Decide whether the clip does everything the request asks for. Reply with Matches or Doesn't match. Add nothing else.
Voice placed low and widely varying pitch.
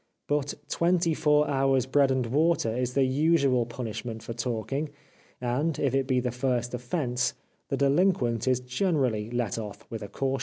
Doesn't match